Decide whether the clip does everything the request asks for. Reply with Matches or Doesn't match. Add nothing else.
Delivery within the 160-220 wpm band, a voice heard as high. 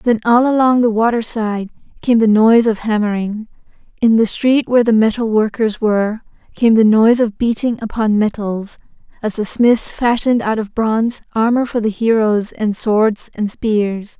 Matches